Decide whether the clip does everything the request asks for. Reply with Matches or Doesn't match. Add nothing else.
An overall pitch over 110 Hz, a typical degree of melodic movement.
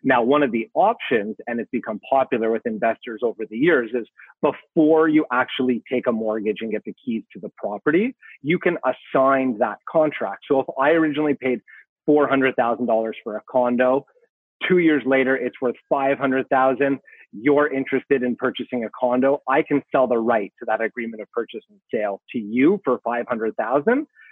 Matches